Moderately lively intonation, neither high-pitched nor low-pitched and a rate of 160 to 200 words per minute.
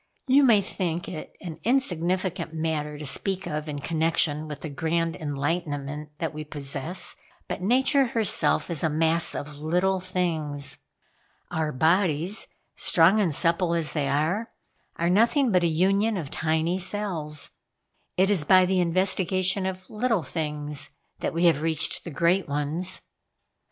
No: average, 3.6 semitones; medium, 170 Hz; average, 150 wpm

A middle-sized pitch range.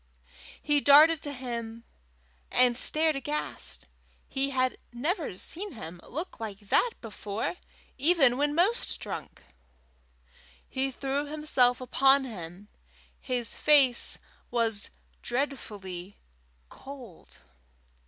Yes: average, 4.4 semitones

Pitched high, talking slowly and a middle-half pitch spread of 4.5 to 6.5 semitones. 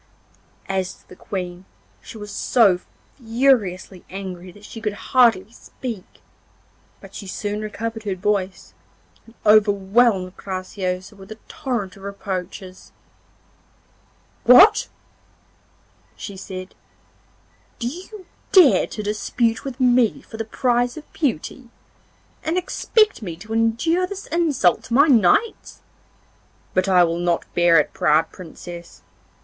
Yes: high, 210 Hz; slow, 125 wpm; average, 4.8 semitones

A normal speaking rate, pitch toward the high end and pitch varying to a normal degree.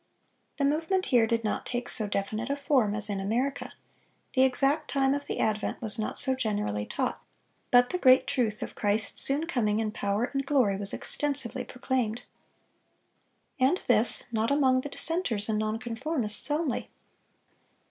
Yes: average, 165 wpm; high, 245 Hz; average, 4.5 semitones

